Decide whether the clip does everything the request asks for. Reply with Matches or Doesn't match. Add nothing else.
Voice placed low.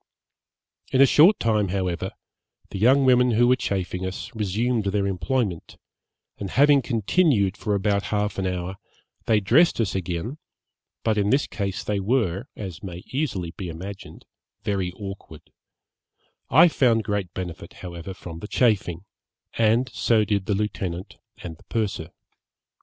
Matches